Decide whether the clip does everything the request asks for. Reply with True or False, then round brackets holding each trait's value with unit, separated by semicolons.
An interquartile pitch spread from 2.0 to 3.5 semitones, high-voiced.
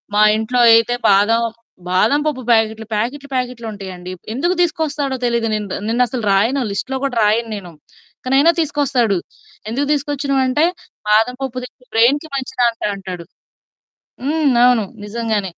False (3.9 semitones; 240 Hz)